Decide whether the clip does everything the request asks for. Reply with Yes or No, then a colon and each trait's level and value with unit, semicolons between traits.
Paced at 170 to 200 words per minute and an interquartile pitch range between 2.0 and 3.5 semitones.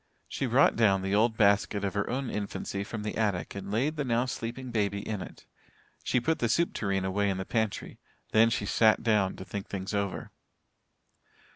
Yes: average, 195 wpm; average, 2.9 semitones